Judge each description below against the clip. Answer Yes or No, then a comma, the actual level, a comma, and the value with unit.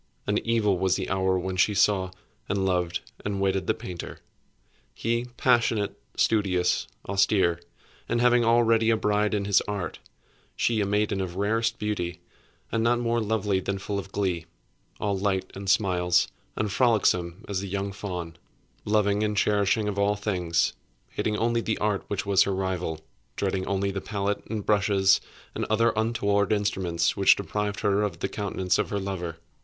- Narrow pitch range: Yes, narrow, 2.0 semitones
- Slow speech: No, average, 165 wpm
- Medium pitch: No, low, 100 Hz